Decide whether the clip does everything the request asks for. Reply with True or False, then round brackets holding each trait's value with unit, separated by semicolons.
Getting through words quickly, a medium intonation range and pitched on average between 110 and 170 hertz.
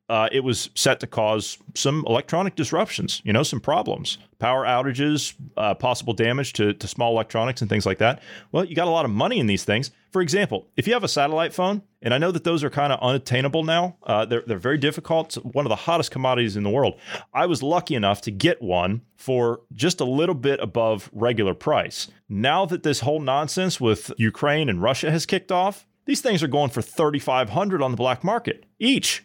False (215 wpm; 6.3 semitones; 140 Hz)